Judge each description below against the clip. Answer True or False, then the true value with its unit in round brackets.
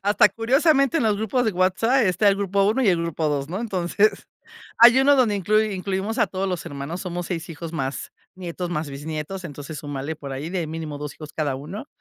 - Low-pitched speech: False (185 Hz)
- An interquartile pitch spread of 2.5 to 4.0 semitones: False (5.4 semitones)